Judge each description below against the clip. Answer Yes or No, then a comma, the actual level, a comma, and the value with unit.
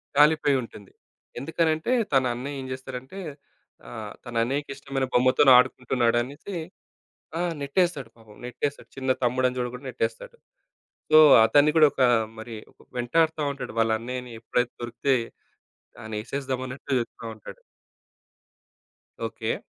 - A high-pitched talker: No, low, 130 Hz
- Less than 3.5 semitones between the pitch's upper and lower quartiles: Yes, average, 2.9 semitones